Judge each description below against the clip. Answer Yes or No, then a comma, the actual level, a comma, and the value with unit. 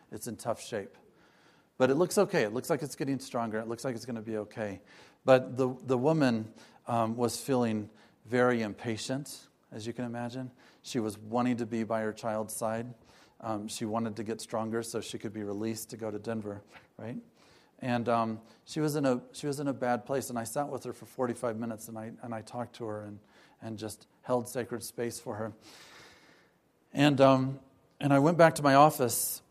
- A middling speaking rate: No, fast, 210 wpm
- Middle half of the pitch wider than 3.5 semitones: No, average, 2.7 semitones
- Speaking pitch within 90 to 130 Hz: Yes, low, 120 Hz